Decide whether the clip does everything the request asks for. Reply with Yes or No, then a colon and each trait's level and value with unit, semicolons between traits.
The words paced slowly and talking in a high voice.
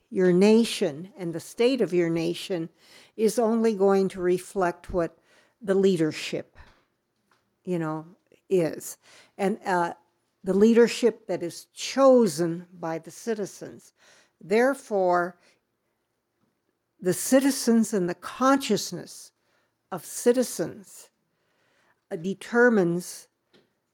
Yes: slow, 95 wpm; high, 195 Hz